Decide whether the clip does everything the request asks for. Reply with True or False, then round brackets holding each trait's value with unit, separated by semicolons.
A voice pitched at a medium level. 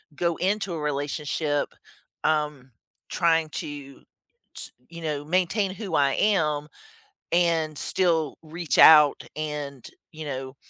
True (155 Hz)